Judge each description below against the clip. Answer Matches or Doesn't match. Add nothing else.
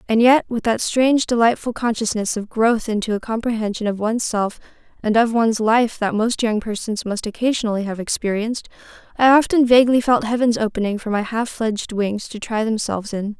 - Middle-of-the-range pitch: Doesn't match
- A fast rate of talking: Doesn't match